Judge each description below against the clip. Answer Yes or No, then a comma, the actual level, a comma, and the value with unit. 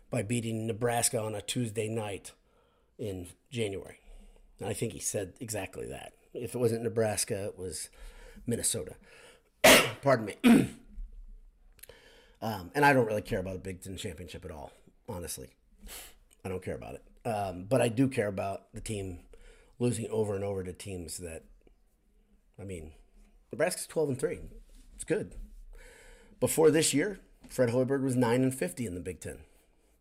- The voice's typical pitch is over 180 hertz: No, low, 110 Hz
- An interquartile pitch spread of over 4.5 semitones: Yes, average, 5.0 semitones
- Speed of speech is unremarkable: Yes, average, 160 wpm